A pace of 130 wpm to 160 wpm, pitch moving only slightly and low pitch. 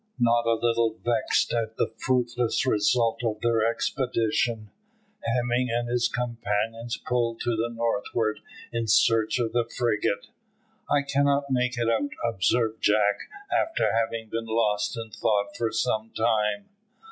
Yes: average, 140 wpm; narrow, 1.5 semitones; low, 115 Hz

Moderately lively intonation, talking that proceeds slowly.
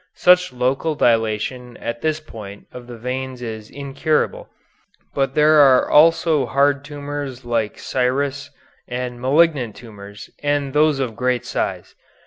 Yes: average, 3.2 semitones; slow, 130 wpm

